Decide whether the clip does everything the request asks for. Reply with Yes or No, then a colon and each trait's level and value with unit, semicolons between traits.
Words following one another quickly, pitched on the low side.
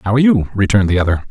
Yes: fast, 275 wpm; low, 105 Hz